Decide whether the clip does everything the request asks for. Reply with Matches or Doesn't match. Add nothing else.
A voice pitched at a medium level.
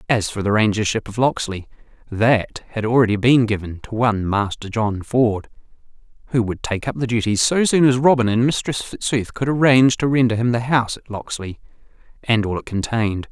Doesn't match